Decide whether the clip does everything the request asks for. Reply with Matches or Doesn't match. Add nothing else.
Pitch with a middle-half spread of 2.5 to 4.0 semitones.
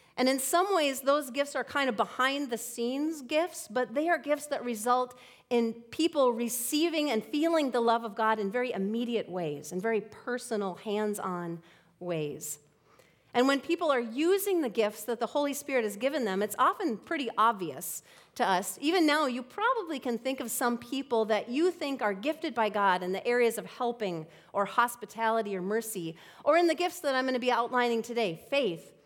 Doesn't match